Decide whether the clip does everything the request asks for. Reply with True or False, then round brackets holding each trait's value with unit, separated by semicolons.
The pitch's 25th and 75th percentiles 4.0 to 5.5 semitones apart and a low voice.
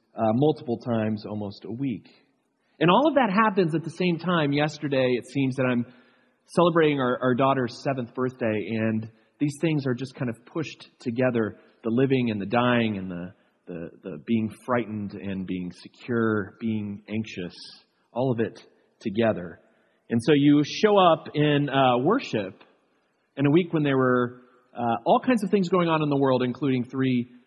True (4.7 semitones; 125 Hz)